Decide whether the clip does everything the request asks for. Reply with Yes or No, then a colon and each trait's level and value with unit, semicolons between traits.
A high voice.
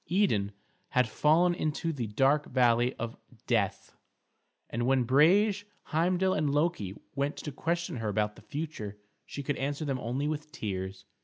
No: medium, 140 Hz